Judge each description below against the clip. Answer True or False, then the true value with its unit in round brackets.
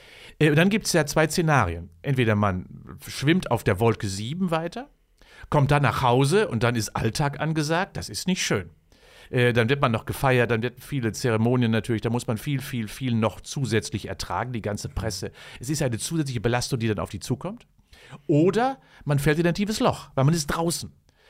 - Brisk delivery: True (200 wpm)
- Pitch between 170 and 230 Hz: False (125 Hz)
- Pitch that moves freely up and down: True (5.9 semitones)